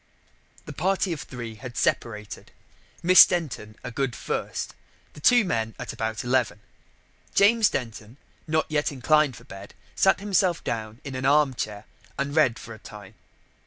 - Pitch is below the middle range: Yes, low, 130 Hz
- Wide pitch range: Yes, wide, 5.7 semitones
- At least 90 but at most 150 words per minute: No, average, 160 wpm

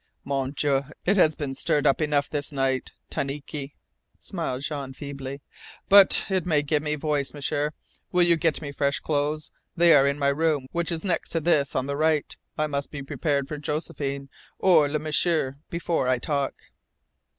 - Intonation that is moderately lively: No, narrow, 2.1 semitones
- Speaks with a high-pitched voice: No, medium, 145 Hz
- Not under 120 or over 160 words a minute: No, average, 180 wpm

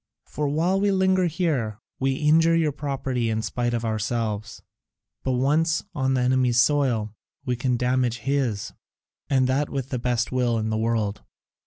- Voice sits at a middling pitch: No, low, 130 Hz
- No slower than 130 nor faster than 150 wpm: No, average, 165 wpm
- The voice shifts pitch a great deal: No, average, 3.9 semitones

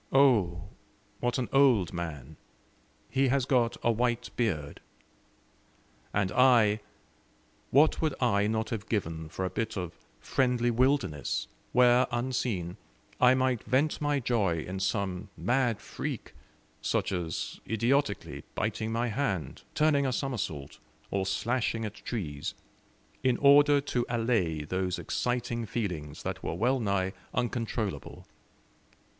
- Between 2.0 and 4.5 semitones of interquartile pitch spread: No, average, 5.1 semitones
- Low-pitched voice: Yes, low, 115 Hz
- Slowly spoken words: Yes, slow, 125 wpm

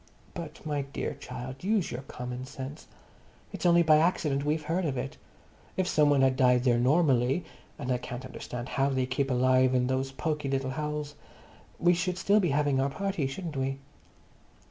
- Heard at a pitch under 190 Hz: Yes, low, 135 Hz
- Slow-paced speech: No, average, 175 wpm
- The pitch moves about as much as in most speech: Yes, average, 3.2 semitones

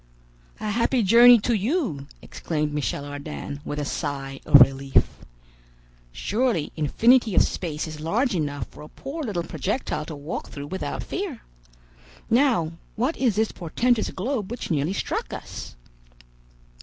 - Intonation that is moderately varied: No, wide, 8.3 semitones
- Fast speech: No, average, 145 wpm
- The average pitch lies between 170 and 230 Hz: Yes, medium, 185 Hz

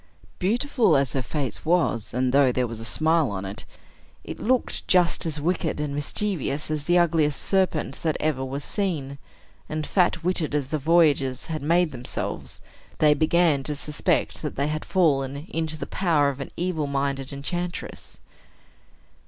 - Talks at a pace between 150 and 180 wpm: Yes, average, 165 wpm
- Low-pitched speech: No, medium, 150 Hz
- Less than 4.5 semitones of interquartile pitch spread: Yes, average, 3.7 semitones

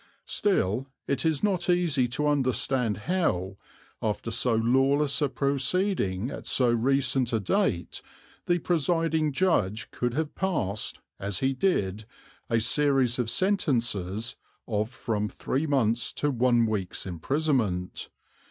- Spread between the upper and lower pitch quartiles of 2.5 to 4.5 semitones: No, average, 5.2 semitones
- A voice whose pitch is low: Yes, low, 130 Hz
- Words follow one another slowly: Yes, slow, 125 wpm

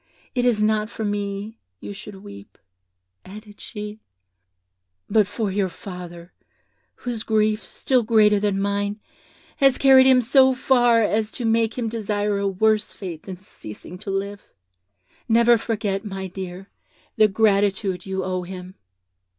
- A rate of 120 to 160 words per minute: Yes, average, 140 wpm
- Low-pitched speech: No, high, 210 Hz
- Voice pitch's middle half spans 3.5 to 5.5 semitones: No, narrow, 2.5 semitones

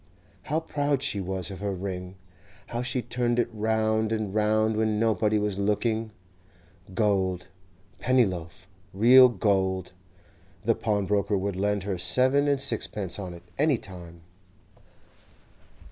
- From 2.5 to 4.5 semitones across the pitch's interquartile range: Yes, average, 3.7 semitones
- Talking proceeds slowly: Yes, slow, 130 wpm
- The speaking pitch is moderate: No, low, 105 Hz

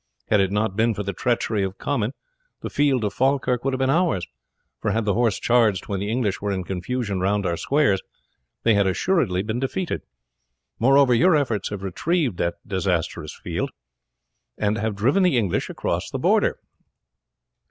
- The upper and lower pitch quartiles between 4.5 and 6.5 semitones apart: Yes, average, 4.9 semitones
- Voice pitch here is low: Yes, low, 110 Hz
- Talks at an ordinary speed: Yes, average, 175 wpm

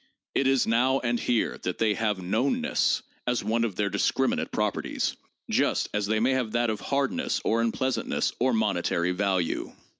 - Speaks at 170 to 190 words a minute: Yes, average, 175 wpm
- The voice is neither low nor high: No, low, 115 Hz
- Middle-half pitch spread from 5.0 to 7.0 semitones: No, average, 3.4 semitones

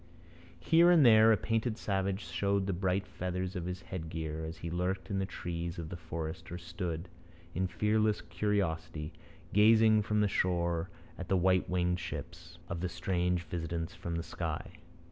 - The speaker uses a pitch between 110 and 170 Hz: No, very low, 90 Hz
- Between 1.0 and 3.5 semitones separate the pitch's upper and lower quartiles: Yes, average, 2.9 semitones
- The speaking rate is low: No, average, 170 wpm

